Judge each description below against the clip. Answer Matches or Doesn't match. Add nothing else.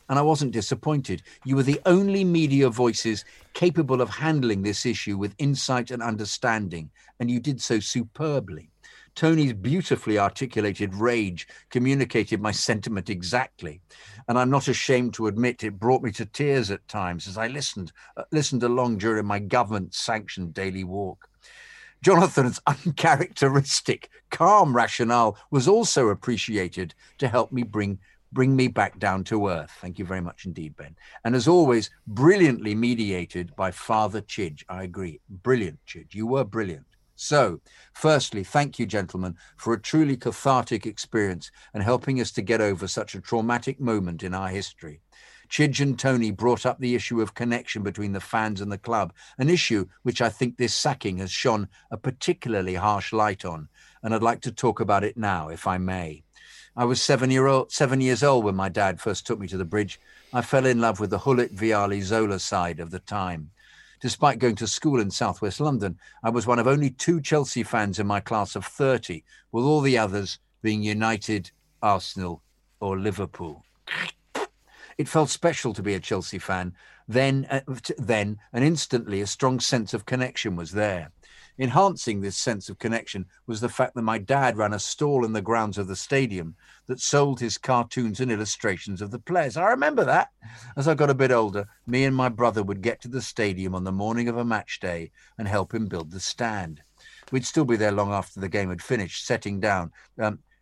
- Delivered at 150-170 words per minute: Doesn't match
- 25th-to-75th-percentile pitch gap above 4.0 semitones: Matches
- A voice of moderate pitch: Doesn't match